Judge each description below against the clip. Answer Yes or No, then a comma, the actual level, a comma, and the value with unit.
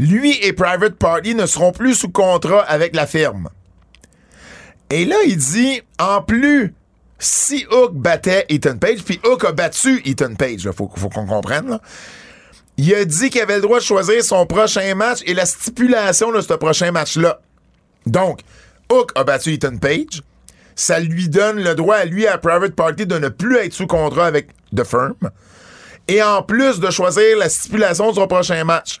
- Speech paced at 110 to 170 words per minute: No, average, 190 wpm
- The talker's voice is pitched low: No, medium, 185 Hz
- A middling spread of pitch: No, wide, 5.9 semitones